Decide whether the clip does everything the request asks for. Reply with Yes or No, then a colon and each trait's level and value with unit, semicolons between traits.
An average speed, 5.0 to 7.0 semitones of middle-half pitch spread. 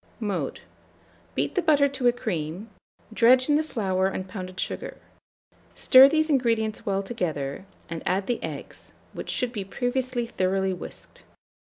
Yes: average, 150 wpm; average, 5.3 semitones